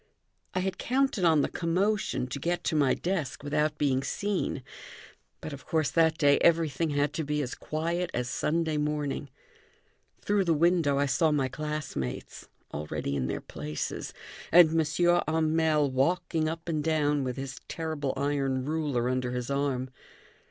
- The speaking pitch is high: No, medium, 150 Hz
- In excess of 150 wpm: Yes, average, 160 wpm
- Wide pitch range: No, average, 3.2 semitones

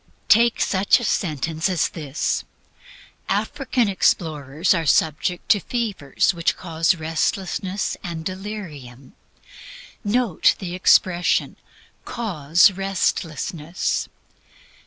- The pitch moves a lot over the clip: No, average, 4.0 semitones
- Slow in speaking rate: Yes, slow, 90 wpm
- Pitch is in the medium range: Yes, medium, 175 Hz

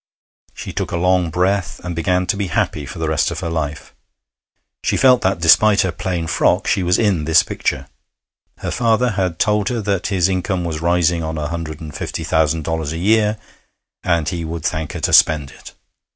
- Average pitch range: Yes, average, 3.2 semitones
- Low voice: Yes, very low, 85 Hz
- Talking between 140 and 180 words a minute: No, fast, 205 wpm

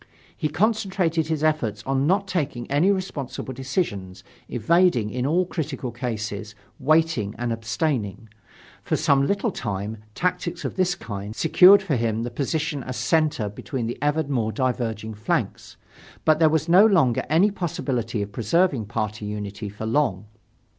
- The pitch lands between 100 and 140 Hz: Yes, low, 135 Hz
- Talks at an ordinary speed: Yes, average, 150 wpm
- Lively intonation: Yes, wide, 6.7 semitones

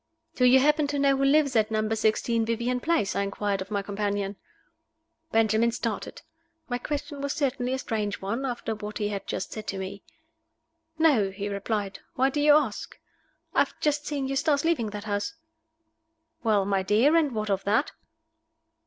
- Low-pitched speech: No, high, 225 Hz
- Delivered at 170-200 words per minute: Yes, average, 180 wpm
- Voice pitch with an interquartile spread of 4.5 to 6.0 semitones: Yes, average, 5.3 semitones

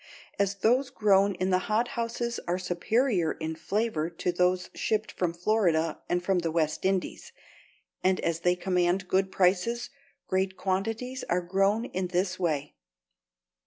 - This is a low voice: No, medium, 185 Hz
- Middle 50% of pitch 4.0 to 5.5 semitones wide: No, average, 3.4 semitones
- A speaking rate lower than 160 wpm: Yes, average, 145 wpm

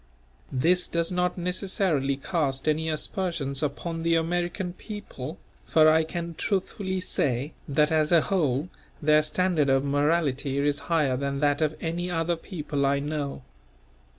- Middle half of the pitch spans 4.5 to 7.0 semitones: No, average, 3.6 semitones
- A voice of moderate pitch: Yes, medium, 155 Hz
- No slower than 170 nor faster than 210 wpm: No, average, 145 wpm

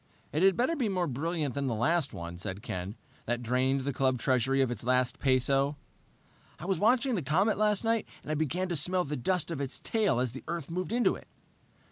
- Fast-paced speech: Yes, fast, 220 wpm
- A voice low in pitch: No, medium, 145 Hz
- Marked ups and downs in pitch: Yes, wide, 6.3 semitones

